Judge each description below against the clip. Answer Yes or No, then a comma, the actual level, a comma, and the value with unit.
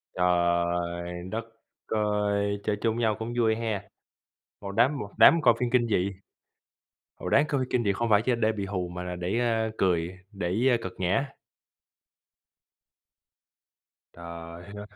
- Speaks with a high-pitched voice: No, low, 100 Hz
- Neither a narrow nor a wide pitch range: Yes, average, 4.5 semitones